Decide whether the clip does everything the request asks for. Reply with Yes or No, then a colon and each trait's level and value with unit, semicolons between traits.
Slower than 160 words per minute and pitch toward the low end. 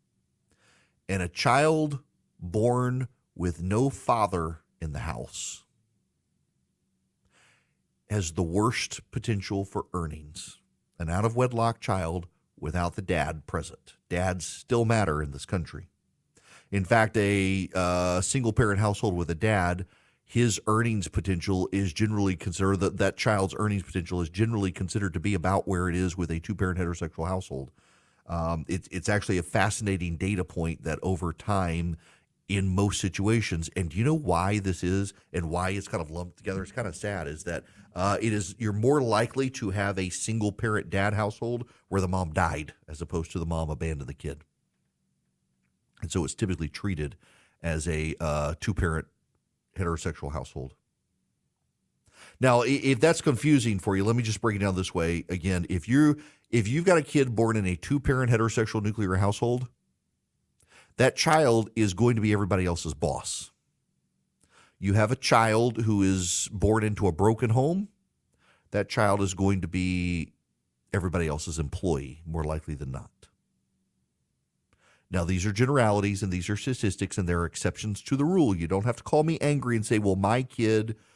No: average, 170 wpm; very low, 95 Hz